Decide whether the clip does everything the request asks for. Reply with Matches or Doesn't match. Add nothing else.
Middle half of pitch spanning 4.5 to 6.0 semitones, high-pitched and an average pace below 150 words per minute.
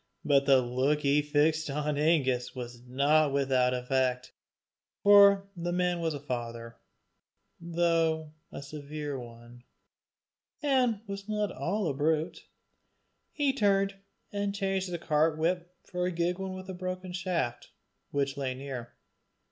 Doesn't match